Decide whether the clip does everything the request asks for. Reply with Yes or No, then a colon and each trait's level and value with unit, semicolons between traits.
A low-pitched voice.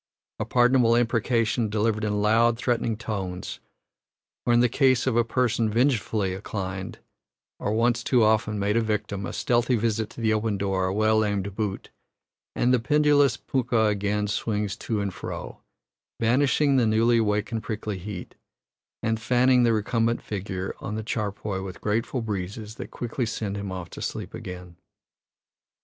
Yes: low, 110 Hz